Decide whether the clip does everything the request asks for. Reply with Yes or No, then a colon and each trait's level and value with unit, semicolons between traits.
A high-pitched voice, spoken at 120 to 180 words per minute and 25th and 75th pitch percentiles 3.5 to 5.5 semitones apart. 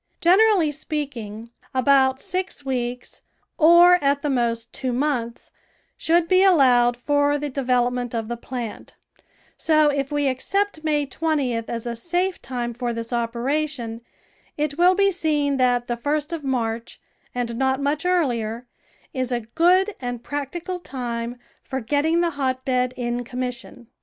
Yes: very high, 265 Hz; average, 150 wpm; average, 4.2 semitones